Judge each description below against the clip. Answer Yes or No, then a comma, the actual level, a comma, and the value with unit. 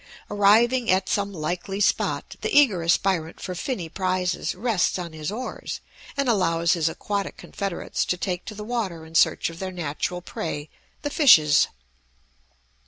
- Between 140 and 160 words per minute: Yes, average, 155 wpm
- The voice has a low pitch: No, medium, 185 Hz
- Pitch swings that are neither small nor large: Yes, average, 3.8 semitones